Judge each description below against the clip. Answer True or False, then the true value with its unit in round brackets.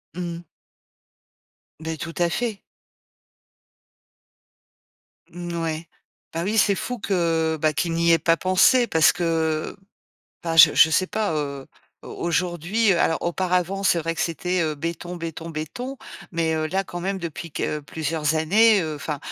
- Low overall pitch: False (170 Hz)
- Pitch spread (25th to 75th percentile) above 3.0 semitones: False (2.4 semitones)